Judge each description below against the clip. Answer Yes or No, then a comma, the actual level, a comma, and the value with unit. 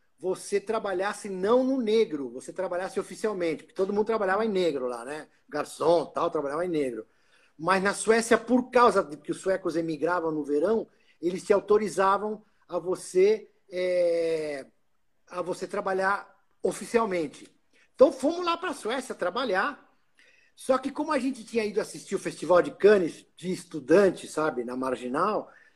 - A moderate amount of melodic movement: Yes, average, 4.9 semitones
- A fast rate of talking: No, average, 155 wpm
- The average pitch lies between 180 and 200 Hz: Yes, high, 190 Hz